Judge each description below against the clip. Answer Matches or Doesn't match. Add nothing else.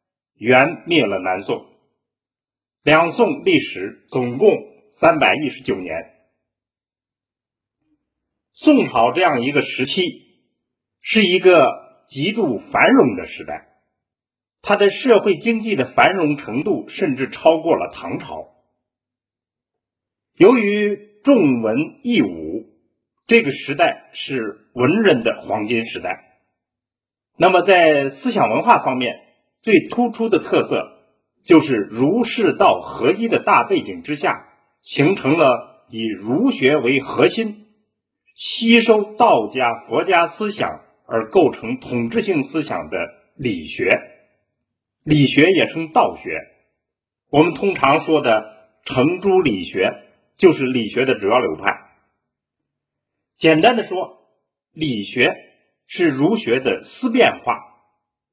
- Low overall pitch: Doesn't match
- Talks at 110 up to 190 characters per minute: Matches